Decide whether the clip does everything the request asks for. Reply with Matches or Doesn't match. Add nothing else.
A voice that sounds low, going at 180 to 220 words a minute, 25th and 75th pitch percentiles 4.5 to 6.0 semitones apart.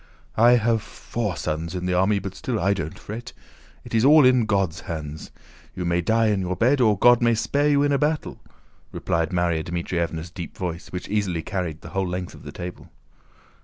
Matches